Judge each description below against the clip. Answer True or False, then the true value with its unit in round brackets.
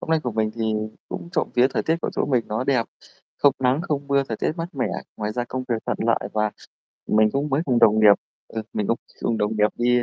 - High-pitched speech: False (120 Hz)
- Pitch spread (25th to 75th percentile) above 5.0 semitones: False (4.2 semitones)